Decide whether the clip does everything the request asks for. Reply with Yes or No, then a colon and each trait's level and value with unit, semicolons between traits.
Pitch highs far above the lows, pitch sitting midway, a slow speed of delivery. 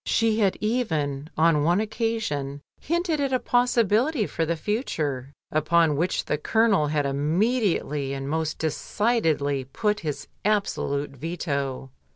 Yes: wide, 7.3 semitones; medium, 165 Hz; slow, 130 wpm